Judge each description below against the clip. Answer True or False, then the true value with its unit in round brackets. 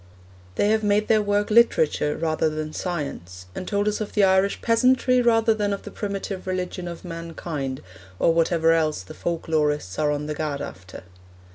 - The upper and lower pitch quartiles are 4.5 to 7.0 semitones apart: True (5.2 semitones)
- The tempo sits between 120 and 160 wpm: False (180 wpm)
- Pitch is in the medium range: True (175 Hz)